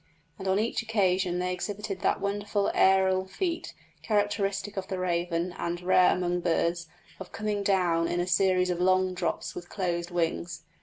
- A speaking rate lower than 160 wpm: No, average, 165 wpm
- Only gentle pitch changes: Yes, narrow, 2.2 semitones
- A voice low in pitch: No, medium, 185 Hz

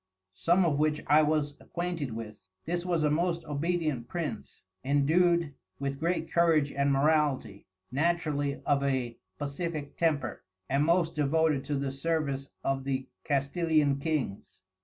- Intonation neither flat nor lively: Yes, average, 3.1 semitones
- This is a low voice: No, medium, 150 Hz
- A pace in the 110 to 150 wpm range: Yes, average, 140 wpm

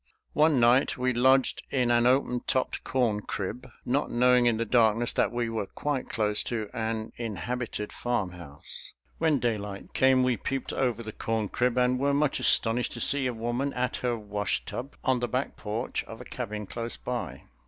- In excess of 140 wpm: Yes, average, 185 wpm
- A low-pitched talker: Yes, low, 120 Hz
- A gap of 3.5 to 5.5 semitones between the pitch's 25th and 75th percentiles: No, narrow, 2.6 semitones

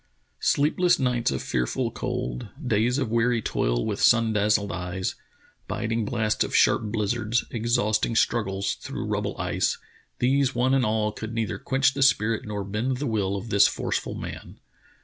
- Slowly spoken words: No, average, 170 wpm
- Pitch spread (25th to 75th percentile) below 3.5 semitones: Yes, average, 2.9 semitones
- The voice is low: Yes, low, 110 Hz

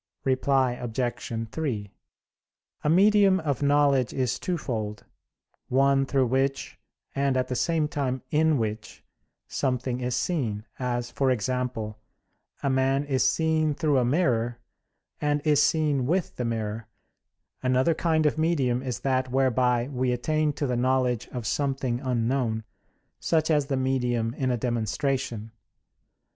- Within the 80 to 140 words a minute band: Yes, slow, 135 wpm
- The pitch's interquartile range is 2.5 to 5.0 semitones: Yes, average, 3.1 semitones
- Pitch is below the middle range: Yes, low, 130 Hz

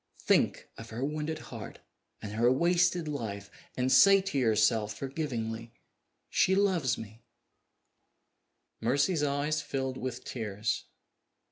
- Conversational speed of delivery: No, slow, 115 wpm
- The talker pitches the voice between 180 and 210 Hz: No, low, 130 Hz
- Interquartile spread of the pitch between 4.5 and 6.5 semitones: Yes, average, 5.3 semitones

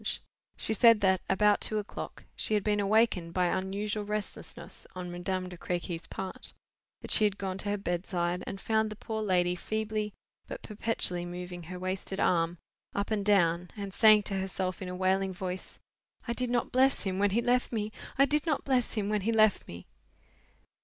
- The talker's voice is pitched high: Yes, high, 200 Hz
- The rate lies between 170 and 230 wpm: Yes, average, 185 wpm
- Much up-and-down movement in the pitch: No, average, 2.9 semitones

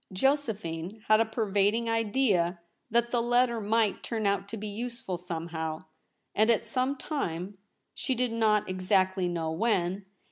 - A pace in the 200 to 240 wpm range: No, average, 145 wpm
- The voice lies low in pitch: No, high, 210 Hz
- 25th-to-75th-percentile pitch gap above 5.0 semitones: No, average, 4.1 semitones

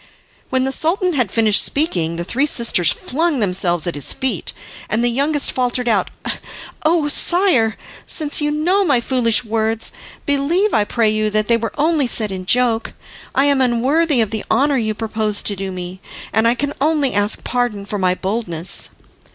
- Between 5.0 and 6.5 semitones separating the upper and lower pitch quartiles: Yes, average, 5.3 semitones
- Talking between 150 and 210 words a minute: Yes, average, 180 wpm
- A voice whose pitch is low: No, high, 235 Hz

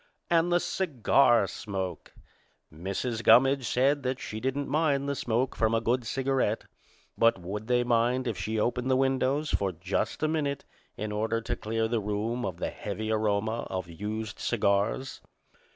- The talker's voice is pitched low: Yes, low, 115 Hz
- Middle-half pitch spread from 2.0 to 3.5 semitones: No, average, 4.0 semitones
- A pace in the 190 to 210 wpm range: No, average, 165 wpm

